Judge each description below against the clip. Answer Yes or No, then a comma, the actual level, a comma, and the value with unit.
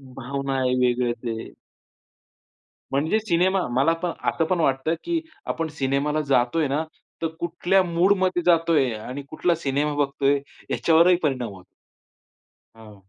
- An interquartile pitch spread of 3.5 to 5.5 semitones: Yes, average, 4.2 semitones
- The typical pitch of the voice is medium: Yes, medium, 150 Hz